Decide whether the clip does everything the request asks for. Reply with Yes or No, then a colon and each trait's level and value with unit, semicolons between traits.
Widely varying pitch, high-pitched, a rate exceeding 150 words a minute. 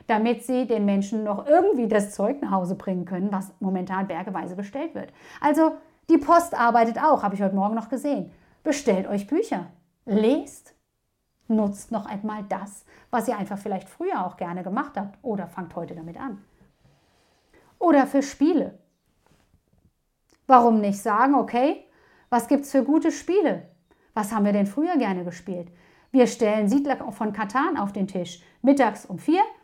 Yes: wide, 5.8 semitones; high, 220 Hz; average, 165 wpm